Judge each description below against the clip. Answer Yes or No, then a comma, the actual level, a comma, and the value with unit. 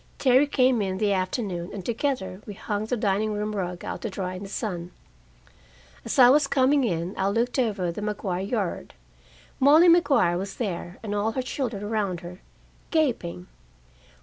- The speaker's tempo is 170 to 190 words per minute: Yes, average, 175 wpm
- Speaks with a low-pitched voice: No, high, 210 Hz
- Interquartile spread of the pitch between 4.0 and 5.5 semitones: Yes, average, 5.0 semitones